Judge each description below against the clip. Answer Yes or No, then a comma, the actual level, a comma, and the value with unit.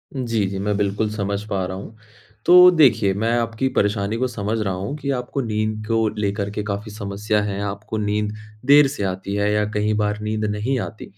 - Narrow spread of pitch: Yes, narrow, 2.0 semitones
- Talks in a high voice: No, low, 105 Hz